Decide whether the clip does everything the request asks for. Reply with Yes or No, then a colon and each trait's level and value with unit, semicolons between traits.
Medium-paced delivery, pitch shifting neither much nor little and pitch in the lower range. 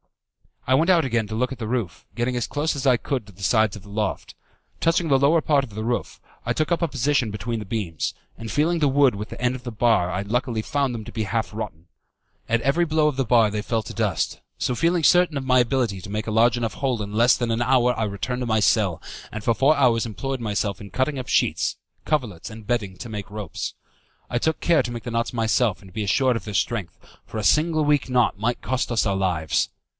No: fast, 255 wpm; average, 3.9 semitones; low, 120 Hz